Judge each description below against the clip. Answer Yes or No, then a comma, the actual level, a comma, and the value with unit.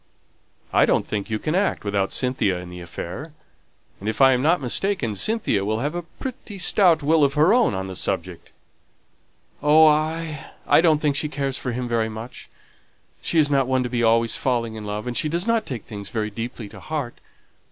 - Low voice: Yes, low, 130 Hz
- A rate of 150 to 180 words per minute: No, fast, 205 wpm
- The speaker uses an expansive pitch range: Yes, wide, 6.2 semitones